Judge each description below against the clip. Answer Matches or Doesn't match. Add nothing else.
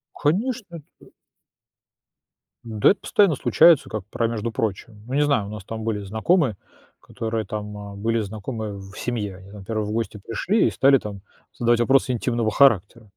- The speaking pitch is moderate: Doesn't match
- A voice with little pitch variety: Doesn't match